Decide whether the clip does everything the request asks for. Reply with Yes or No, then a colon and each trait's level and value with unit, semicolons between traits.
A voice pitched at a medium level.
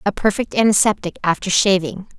No: high, 200 Hz